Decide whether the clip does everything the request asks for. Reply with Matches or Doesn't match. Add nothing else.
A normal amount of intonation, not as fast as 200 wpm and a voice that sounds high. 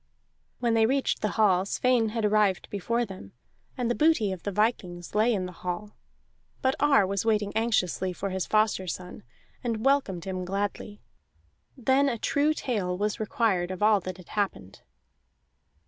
Matches